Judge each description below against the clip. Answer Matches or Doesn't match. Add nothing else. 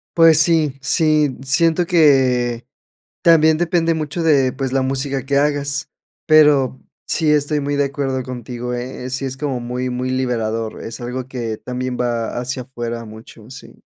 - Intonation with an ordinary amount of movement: Matches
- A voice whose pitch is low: Matches